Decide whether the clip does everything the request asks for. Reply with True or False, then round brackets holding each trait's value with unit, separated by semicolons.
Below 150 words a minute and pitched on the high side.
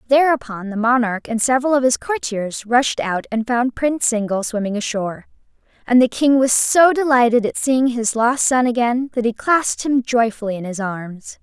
False (190 wpm; 240 Hz)